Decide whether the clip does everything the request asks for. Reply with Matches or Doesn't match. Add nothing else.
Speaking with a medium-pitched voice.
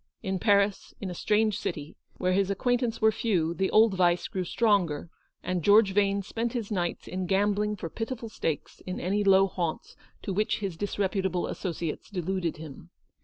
Doesn't match